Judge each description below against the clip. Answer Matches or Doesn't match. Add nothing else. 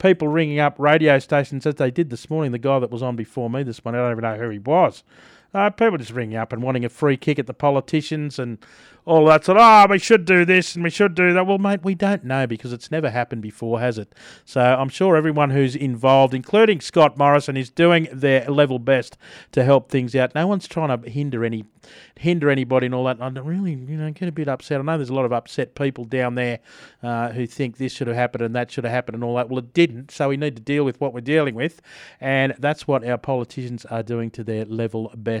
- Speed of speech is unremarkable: Doesn't match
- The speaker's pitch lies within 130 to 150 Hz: Matches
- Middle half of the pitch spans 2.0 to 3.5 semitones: Doesn't match